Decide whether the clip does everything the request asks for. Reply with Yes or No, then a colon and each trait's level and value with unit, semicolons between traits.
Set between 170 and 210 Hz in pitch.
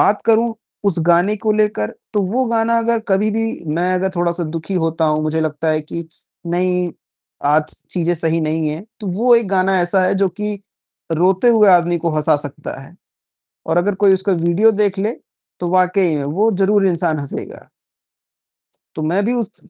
Yes: medium, 185 Hz